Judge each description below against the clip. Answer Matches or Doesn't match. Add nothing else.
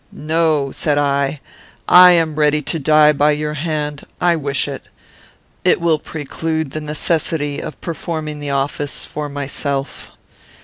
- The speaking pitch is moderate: Matches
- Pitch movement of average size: Doesn't match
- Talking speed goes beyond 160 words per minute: Doesn't match